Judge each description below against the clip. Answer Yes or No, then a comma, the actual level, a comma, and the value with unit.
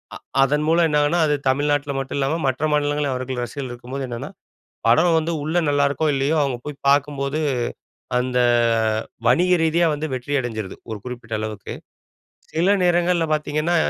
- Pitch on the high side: No, medium, 145 Hz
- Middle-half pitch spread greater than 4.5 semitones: No, average, 3.4 semitones